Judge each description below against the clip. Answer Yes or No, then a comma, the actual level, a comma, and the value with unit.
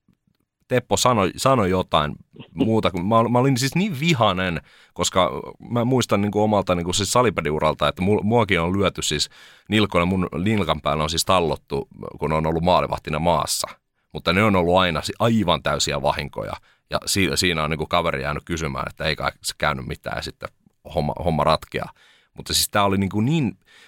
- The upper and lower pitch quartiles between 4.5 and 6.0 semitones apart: Yes, average, 5.2 semitones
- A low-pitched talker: Yes, very low, 95 Hz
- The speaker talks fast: Yes, fast, 175 wpm